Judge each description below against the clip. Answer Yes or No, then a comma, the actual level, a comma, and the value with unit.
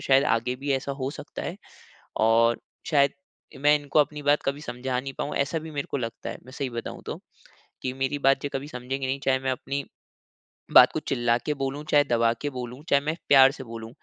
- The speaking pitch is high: No, low, 135 Hz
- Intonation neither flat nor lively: No, narrow, 2.3 semitones